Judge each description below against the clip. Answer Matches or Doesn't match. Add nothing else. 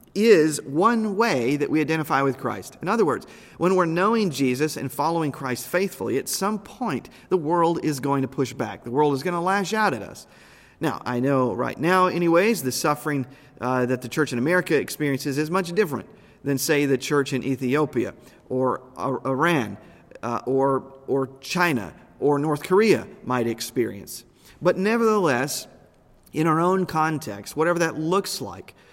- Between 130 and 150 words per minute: Doesn't match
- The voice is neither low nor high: Matches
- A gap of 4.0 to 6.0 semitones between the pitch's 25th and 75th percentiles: Matches